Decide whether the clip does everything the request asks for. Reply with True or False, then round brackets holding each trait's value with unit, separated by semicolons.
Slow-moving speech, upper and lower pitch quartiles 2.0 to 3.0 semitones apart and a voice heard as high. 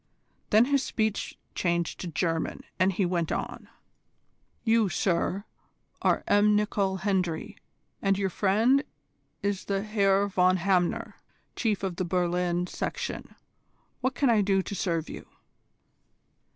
True (130 wpm; 2.7 semitones; 195 Hz)